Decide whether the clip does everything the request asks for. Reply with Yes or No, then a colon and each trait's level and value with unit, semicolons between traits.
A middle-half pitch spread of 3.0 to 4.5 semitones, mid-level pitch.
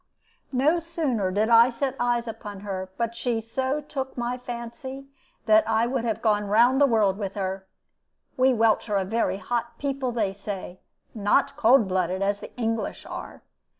No: average, 3.9 semitones; high, 230 Hz